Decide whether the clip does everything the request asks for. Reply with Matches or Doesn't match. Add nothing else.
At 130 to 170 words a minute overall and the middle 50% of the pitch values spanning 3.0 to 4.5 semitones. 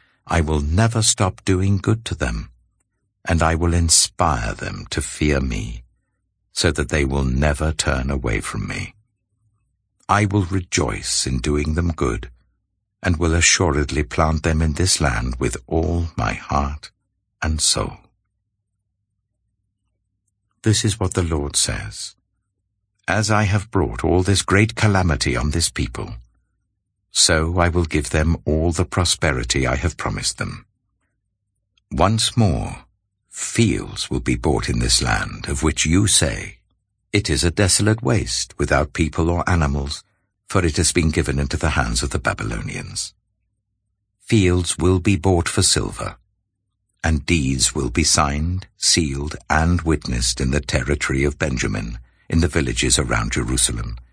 Doesn't match